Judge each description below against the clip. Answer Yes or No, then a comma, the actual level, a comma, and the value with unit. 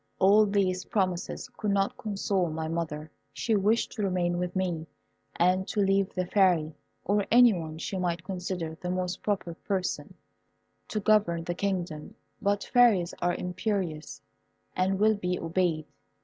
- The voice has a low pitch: No, medium, 185 Hz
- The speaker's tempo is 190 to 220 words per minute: No, average, 150 wpm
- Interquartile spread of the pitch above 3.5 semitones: No, average, 2.7 semitones